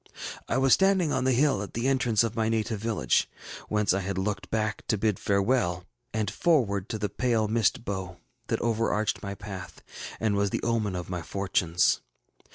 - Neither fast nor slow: Yes, average, 185 wpm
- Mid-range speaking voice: No, low, 110 Hz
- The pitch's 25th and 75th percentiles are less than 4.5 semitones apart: Yes, average, 2.9 semitones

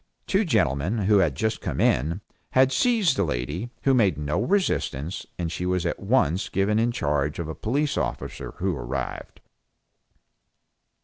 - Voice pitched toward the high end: No, very low, 95 Hz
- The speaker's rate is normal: Yes, average, 160 wpm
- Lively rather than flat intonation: Yes, wide, 7.9 semitones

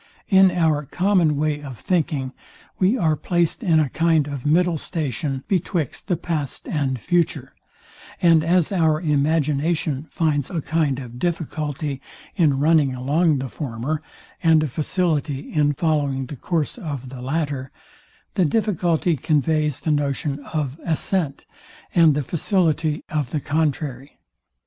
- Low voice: No, medium, 155 Hz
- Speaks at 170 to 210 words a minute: No, average, 140 wpm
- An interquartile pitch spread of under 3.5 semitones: Yes, average, 3.0 semitones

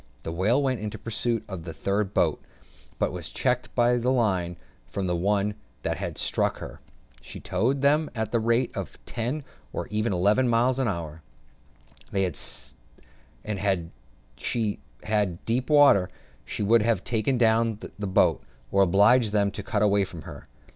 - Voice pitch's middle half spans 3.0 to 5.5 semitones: Yes, average, 3.6 semitones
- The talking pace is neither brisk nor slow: Yes, average, 160 wpm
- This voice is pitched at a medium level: No, low, 105 Hz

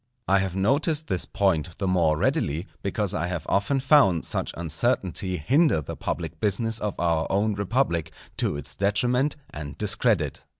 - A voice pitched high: No, low, 100 Hz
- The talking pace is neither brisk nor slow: Yes, average, 160 wpm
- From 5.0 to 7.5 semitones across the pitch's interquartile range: Yes, wide, 5.4 semitones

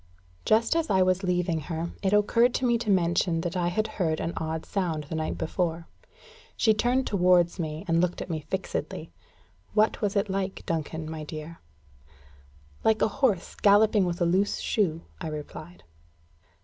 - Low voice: No, medium, 180 Hz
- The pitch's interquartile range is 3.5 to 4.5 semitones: Yes, average, 4.0 semitones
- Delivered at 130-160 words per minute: No, average, 175 wpm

